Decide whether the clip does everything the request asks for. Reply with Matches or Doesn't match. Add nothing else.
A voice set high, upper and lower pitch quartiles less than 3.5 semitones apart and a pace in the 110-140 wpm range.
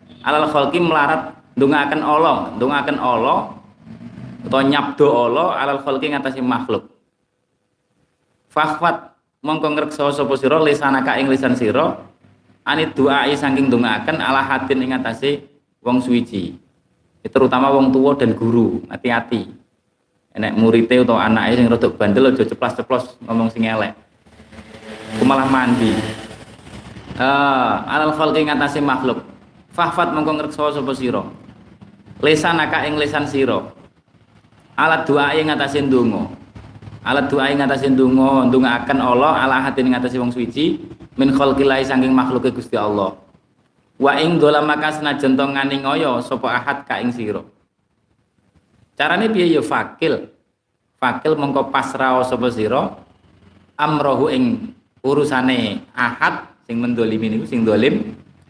Doesn't match